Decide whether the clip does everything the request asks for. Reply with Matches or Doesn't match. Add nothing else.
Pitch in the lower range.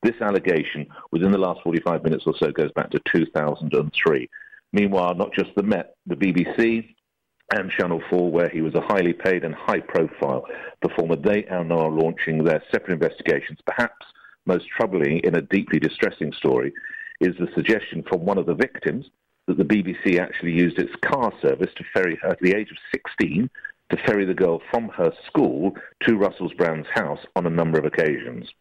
Matches